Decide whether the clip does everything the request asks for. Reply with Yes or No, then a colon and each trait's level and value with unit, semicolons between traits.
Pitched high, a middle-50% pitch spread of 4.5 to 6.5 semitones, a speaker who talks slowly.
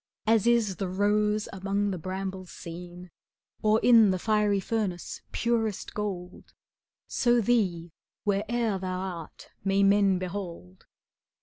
No: high, 195 Hz; average, 2.7 semitones; slow, 125 wpm